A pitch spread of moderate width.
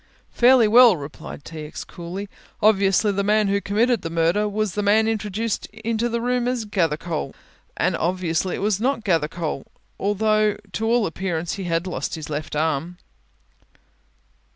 Yes: average, 4.7 semitones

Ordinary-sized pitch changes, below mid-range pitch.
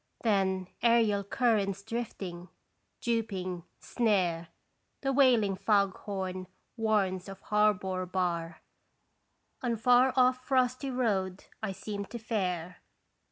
No: average, 4.0 semitones; high, 200 Hz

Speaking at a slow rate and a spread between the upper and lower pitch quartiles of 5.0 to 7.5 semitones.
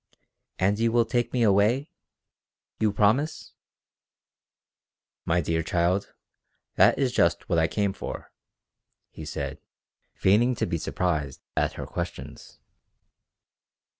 Yes: slow, 115 wpm; wide, 5.6 semitones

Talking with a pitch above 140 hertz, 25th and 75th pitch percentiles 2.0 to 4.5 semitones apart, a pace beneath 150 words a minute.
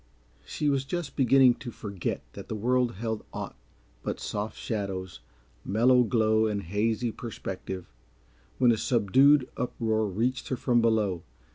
No: low, 115 Hz; average, 3.5 semitones; average, 140 wpm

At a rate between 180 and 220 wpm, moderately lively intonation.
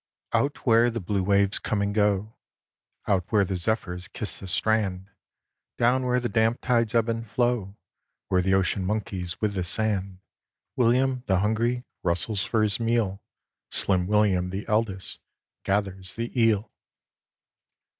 No: average, 145 wpm; average, 3.3 semitones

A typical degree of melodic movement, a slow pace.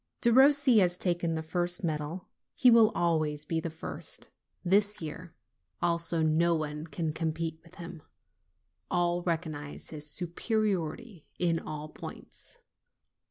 No: narrow, 2.3 semitones; slow, 125 wpm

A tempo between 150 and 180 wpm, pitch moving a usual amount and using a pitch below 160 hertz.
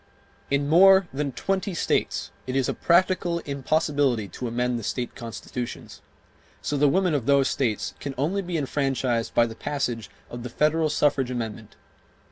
Yes: average, 160 wpm; average, 4.5 semitones; medium, 140 Hz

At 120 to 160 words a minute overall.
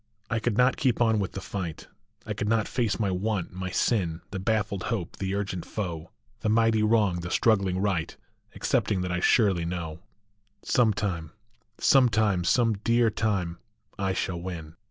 No: average, 175 wpm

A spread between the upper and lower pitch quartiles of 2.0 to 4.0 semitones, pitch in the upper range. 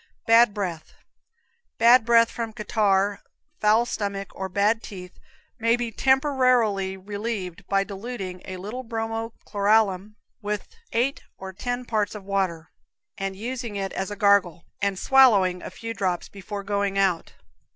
Yes: average, 3.0 semitones; high, 205 Hz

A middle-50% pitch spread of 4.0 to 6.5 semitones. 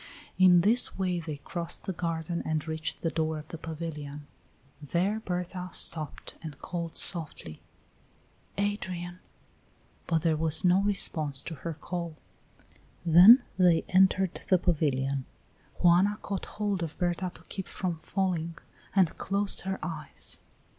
No: average, 2.8 semitones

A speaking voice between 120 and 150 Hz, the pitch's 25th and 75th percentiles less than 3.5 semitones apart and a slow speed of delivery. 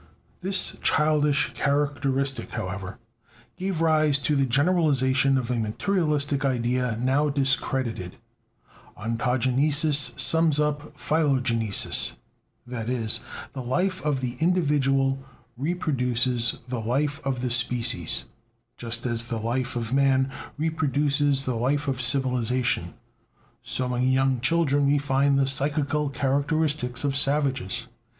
Yes: low, 135 Hz; average, 2.8 semitones; slow, 115 wpm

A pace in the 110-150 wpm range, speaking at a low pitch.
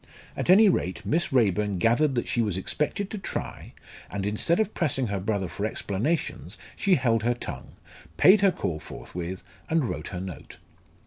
No: average, 175 wpm; low, 115 Hz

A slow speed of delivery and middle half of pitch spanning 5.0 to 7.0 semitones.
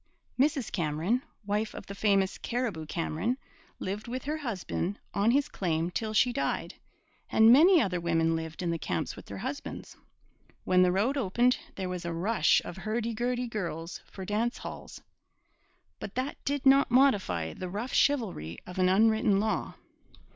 No: average, 165 wpm; wide, 5.5 semitones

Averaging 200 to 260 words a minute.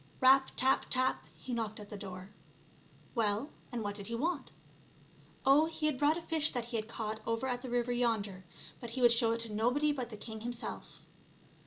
Yes: fast, 205 wpm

